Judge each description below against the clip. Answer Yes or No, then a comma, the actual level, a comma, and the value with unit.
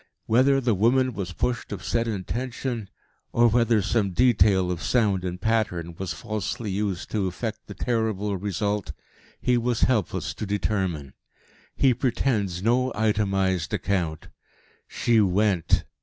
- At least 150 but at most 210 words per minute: No, slow, 135 wpm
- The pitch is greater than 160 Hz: No, low, 105 Hz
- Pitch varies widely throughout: No, average, 3.9 semitones